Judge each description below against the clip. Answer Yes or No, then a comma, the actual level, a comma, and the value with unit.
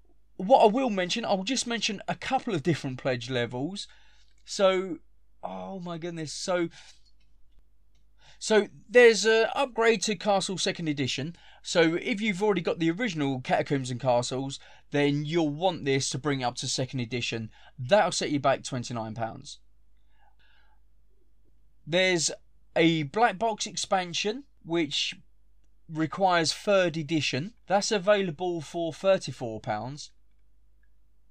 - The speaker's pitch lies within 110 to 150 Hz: No, medium, 165 Hz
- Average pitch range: No, wide, 7.0 semitones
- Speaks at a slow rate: Yes, slow, 125 wpm